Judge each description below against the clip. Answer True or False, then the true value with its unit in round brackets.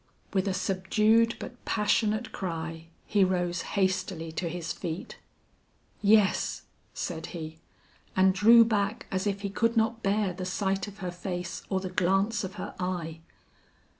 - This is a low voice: False (190 Hz)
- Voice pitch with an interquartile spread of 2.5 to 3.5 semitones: True (2.9 semitones)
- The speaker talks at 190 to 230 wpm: False (150 wpm)